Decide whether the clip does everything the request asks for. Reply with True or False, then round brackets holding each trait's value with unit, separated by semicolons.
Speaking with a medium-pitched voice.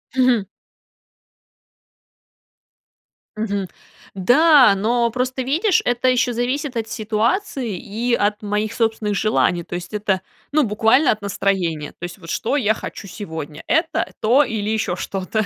False (220 Hz)